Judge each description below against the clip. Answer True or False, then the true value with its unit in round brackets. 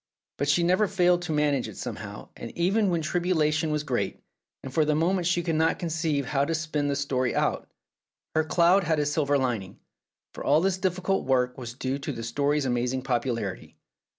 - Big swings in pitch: False (4.3 semitones)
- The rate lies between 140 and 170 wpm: False (195 wpm)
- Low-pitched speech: False (150 Hz)